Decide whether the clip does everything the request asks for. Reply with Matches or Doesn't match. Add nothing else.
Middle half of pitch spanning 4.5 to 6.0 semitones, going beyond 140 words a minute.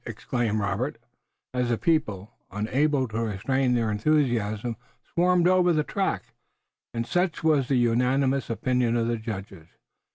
Doesn't match